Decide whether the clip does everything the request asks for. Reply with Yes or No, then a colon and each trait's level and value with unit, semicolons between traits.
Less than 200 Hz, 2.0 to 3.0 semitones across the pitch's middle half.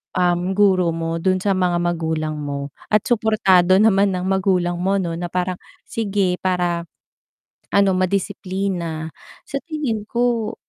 Yes: medium, 185 Hz; narrow, 2.5 semitones